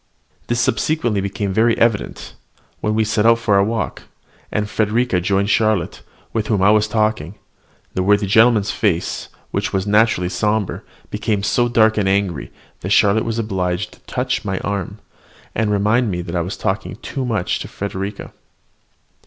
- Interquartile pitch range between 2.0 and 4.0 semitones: Yes, narrow, 2.4 semitones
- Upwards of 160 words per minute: Yes, average, 170 wpm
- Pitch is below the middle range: Yes, low, 105 Hz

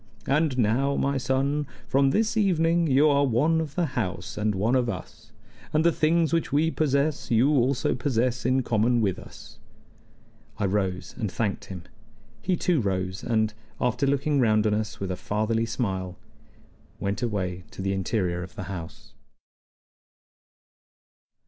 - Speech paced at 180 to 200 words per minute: No, average, 155 wpm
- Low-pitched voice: Yes, low, 120 Hz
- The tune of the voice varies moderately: No, wide, 6.0 semitones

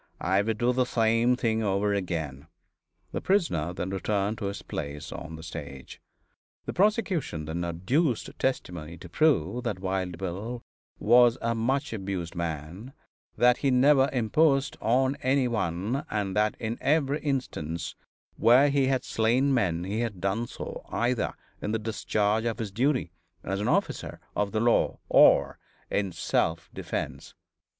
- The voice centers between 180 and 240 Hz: No, low, 110 Hz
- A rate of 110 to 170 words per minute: Yes, average, 155 wpm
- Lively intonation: Yes, wide, 5.7 semitones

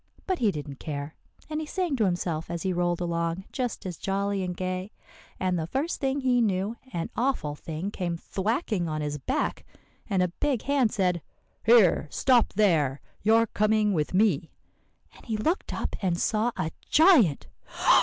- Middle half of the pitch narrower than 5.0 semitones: No, wide, 5.4 semitones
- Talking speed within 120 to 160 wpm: No, average, 175 wpm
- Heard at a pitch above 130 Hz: Yes, high, 190 Hz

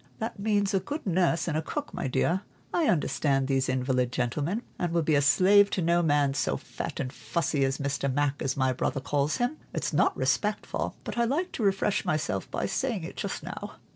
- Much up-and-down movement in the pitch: Yes, wide, 6.3 semitones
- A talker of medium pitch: Yes, medium, 155 Hz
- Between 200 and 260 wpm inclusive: Yes, fast, 205 wpm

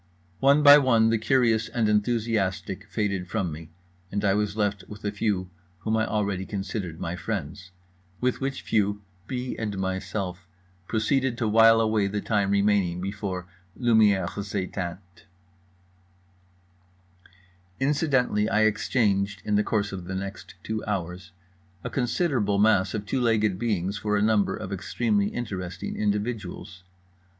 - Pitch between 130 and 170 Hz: No, low, 105 Hz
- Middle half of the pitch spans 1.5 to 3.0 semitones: Yes, narrow, 2.6 semitones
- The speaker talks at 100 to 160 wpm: Yes, average, 140 wpm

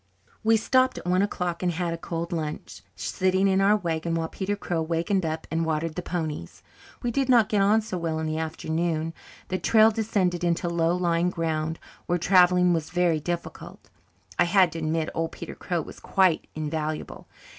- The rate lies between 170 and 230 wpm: Yes, average, 190 wpm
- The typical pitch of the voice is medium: Yes, medium, 170 Hz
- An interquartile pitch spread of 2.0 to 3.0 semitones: Yes, narrow, 2.6 semitones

